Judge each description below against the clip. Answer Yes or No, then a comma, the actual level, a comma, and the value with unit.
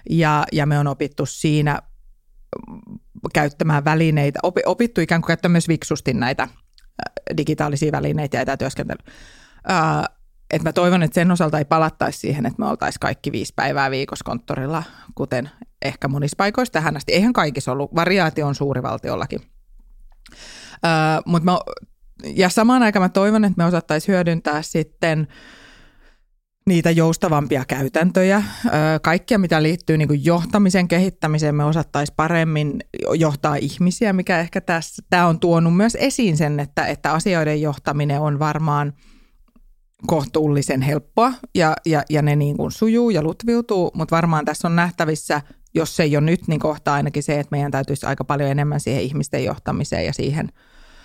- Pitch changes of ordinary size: Yes, average, 3.2 semitones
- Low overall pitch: No, medium, 155 Hz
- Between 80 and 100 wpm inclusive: No, average, 145 wpm